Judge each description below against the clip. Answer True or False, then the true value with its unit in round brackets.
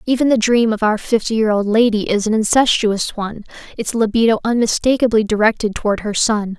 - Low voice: False (220 Hz)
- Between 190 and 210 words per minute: False (180 wpm)